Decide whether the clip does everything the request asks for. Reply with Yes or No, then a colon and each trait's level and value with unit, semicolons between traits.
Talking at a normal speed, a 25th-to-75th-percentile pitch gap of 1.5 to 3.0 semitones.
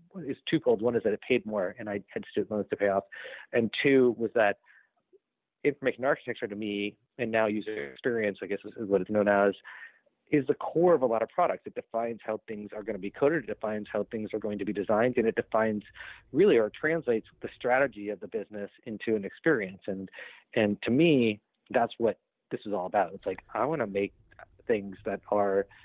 No: fast, 215 wpm; narrow, 2.4 semitones